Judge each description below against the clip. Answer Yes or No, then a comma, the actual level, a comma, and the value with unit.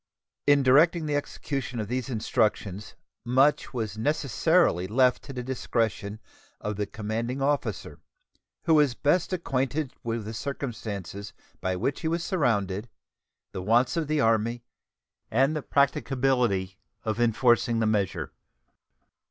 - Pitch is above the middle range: No, low, 120 Hz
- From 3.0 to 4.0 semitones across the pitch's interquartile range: No, average, 4.5 semitones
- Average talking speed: No, slow, 130 wpm